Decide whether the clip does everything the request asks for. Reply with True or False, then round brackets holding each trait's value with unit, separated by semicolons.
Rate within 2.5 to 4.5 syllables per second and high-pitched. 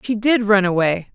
False (4.9 syllables/s; 205 Hz)